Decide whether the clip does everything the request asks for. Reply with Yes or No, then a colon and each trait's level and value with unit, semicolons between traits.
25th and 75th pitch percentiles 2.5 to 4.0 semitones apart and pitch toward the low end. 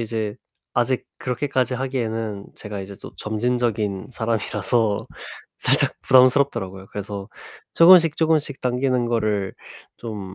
Yes: average, 3.7 semitones; low, 115 Hz